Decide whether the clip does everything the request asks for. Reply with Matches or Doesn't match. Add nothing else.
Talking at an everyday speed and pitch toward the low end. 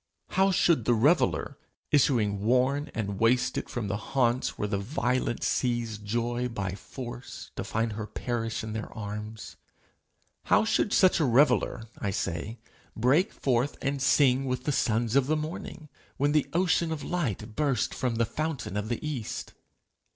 Matches